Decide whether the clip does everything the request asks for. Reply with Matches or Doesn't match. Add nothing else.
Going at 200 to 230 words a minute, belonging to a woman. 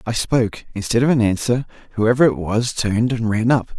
Doesn't match